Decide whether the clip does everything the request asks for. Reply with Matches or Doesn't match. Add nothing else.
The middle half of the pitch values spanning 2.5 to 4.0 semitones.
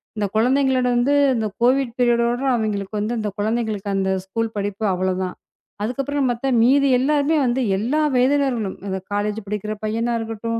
Matches